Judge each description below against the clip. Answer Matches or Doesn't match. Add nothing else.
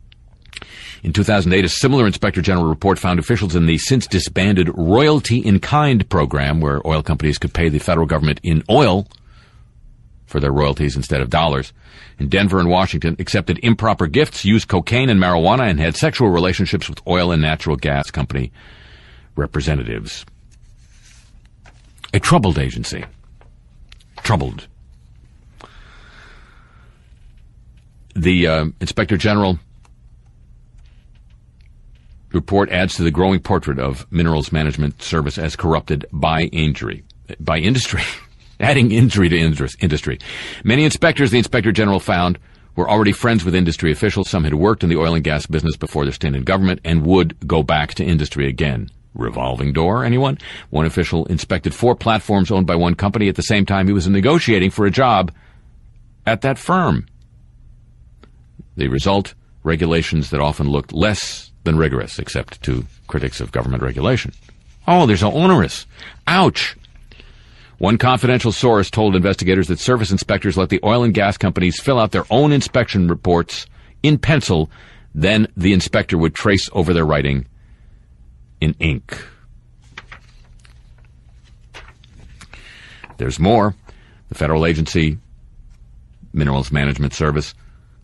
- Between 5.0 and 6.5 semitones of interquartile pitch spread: Matches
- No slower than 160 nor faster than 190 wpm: Doesn't match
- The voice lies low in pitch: Matches